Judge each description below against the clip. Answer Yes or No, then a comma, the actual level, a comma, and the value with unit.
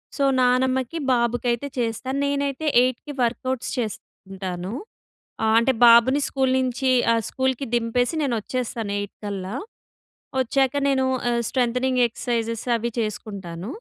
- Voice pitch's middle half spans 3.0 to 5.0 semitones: No, narrow, 2.6 semitones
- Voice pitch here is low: No, high, 245 Hz